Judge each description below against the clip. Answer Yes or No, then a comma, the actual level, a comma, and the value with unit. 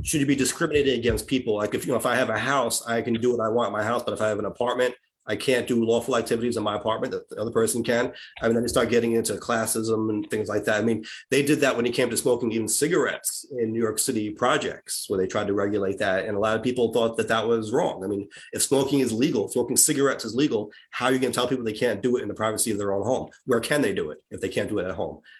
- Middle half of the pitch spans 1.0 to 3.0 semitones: Yes, narrow, 2.6 semitones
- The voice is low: Yes, low, 115 Hz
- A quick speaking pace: Yes, fast, 300 wpm